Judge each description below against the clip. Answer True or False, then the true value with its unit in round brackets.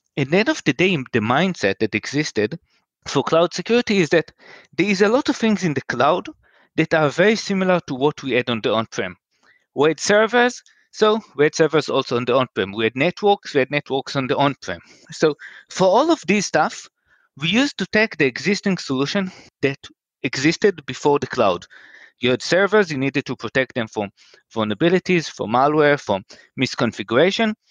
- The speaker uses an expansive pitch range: True (6.3 semitones)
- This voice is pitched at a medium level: True (155 Hz)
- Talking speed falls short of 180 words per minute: False (195 wpm)